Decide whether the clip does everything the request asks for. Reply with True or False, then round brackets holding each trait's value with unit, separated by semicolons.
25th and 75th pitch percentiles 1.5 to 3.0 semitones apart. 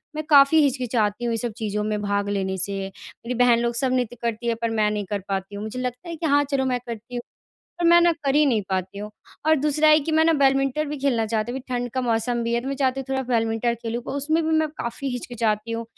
False (4.0 semitones)